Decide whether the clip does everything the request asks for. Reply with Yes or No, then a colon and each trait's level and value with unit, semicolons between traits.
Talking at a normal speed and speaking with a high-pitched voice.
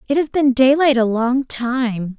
Yes: average, 195 wpm; very high, 255 Hz